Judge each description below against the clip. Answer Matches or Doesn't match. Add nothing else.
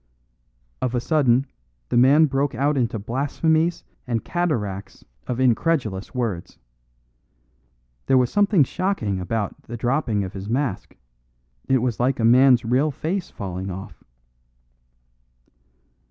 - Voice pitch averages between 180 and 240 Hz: Doesn't match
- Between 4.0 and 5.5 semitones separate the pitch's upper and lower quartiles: Matches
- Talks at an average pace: Doesn't match